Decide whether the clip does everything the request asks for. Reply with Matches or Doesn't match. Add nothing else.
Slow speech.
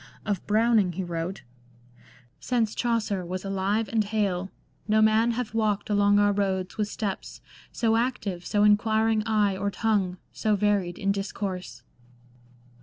Doesn't match